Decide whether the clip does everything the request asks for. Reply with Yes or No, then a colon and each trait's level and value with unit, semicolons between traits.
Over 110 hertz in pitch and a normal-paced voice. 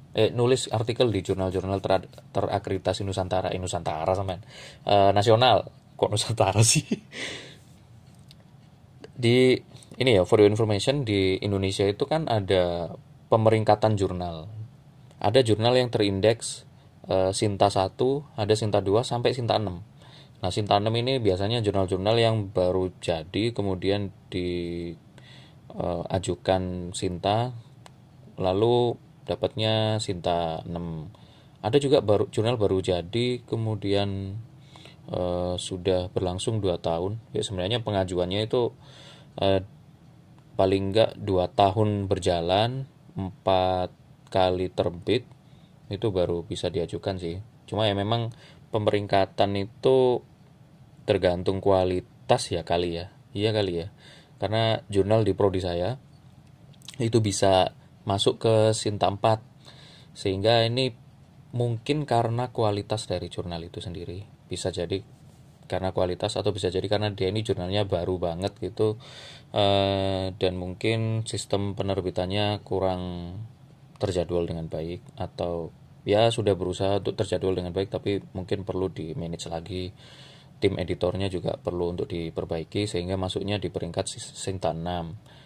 No: low, 105 Hz; average, 120 wpm